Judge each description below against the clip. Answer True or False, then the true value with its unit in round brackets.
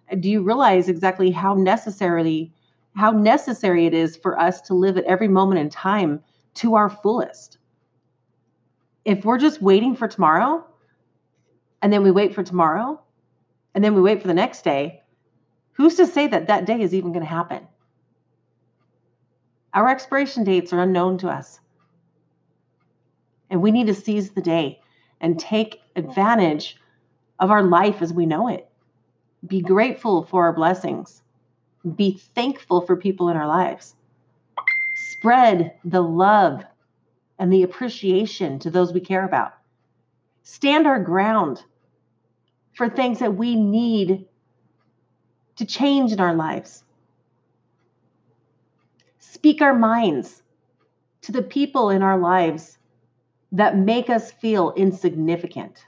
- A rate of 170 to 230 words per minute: False (135 wpm)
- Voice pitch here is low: False (185 Hz)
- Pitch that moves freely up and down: True (5.8 semitones)